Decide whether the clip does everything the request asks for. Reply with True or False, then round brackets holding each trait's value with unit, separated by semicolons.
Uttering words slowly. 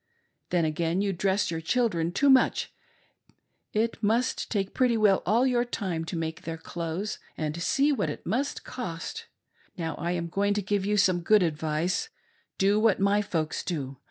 False (170 wpm)